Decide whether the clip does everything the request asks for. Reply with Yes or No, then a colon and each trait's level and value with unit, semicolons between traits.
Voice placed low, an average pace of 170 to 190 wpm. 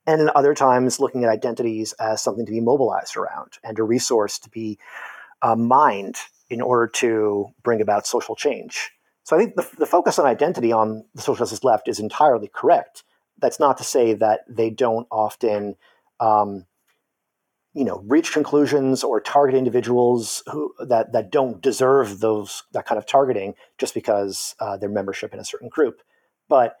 Yes: low, 115 Hz; average, 175 wpm